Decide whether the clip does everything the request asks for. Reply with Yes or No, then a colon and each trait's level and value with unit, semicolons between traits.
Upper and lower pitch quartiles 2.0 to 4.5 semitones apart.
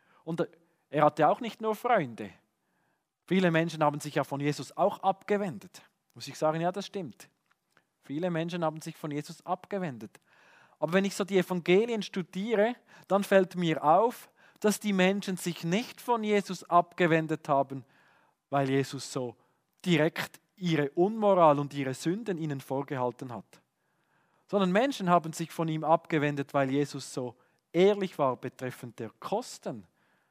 No: average, 5.1 semitones